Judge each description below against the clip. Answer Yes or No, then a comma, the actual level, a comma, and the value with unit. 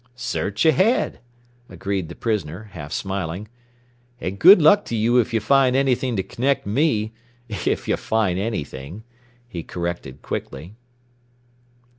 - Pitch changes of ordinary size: No, wide, 5.7 semitones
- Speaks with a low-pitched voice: Yes, low, 110 Hz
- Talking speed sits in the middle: No, slow, 130 wpm